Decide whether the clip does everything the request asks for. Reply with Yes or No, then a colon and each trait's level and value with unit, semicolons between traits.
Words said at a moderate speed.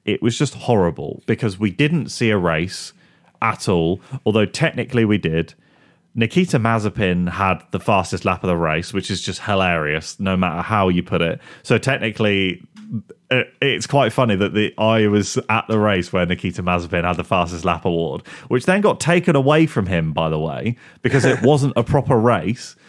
Yes: average, 185 wpm